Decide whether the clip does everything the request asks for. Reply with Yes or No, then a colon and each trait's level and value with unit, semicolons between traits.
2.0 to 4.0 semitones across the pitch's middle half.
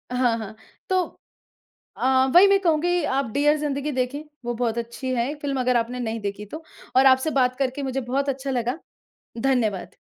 Yes: average, 3.0 semitones